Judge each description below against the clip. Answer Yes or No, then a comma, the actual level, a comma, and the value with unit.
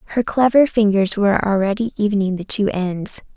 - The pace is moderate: Yes, average, 160 wpm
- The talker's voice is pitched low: No, high, 205 Hz